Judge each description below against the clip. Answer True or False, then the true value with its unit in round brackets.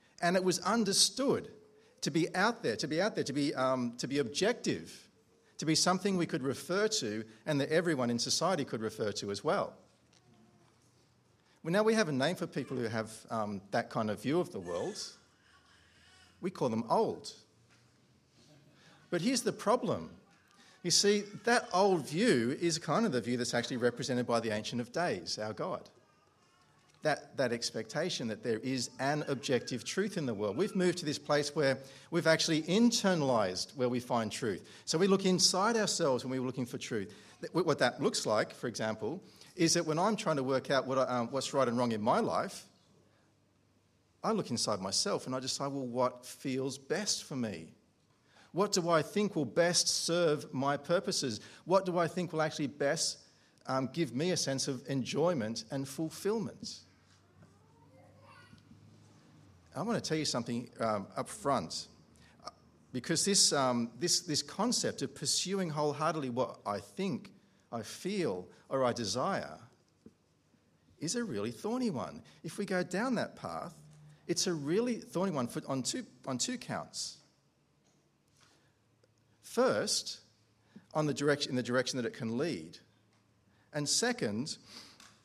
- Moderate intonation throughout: False (6.5 semitones)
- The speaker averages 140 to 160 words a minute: False (170 wpm)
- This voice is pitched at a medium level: True (145 Hz)